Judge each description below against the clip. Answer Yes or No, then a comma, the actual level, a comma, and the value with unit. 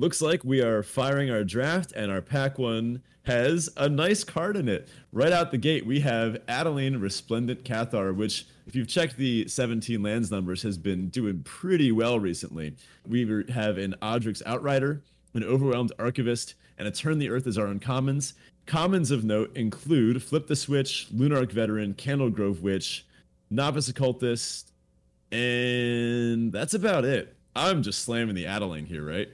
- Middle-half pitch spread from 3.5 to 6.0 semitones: Yes, average, 4.7 semitones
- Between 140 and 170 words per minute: Yes, average, 165 wpm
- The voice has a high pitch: No, low, 120 Hz